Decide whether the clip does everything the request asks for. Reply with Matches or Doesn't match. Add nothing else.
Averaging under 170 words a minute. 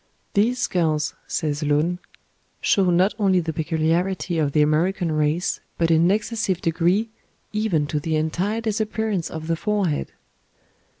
Matches